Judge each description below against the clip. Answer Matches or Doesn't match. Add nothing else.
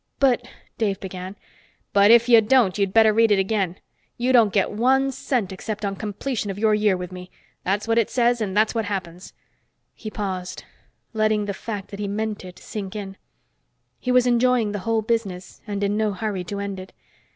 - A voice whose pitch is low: Doesn't match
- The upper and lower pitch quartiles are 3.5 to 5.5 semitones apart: Doesn't match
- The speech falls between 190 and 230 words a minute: Matches